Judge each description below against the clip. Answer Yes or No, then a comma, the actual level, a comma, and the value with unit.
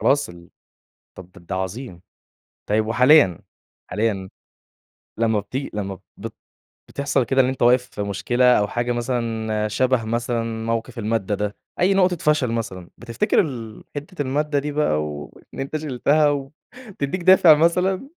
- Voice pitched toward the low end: Yes, low, 120 Hz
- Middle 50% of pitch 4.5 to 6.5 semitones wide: Yes, average, 5.1 semitones